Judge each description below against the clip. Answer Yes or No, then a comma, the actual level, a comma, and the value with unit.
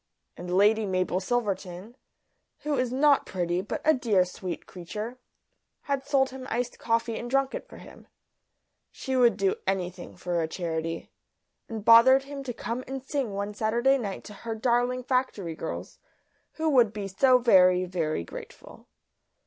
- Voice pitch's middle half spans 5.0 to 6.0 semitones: Yes, wide, 5.6 semitones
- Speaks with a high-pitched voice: Yes, high, 225 Hz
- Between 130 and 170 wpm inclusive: Yes, average, 160 wpm